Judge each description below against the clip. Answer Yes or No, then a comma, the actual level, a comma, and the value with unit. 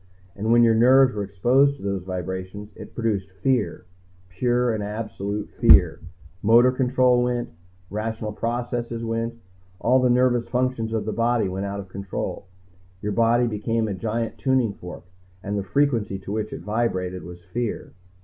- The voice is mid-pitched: No, low, 115 Hz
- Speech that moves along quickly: No, average, 160 wpm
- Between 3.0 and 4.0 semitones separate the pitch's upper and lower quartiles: Yes, average, 3.3 semitones